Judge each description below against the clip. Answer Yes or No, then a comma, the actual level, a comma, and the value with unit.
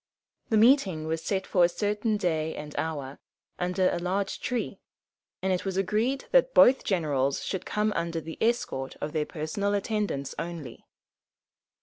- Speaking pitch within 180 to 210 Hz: Yes, medium, 185 Hz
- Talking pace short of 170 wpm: Yes, average, 155 wpm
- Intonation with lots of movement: No, average, 4.9 semitones